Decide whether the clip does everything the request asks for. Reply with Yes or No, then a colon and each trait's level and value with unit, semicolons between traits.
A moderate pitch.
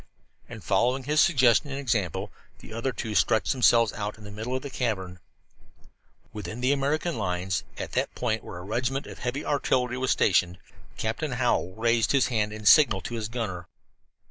No: low, 115 Hz